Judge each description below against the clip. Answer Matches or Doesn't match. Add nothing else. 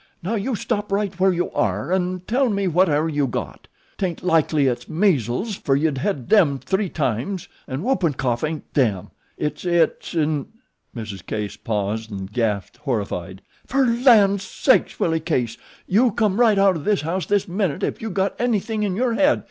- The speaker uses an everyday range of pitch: Doesn't match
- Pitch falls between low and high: Matches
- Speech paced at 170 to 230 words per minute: Matches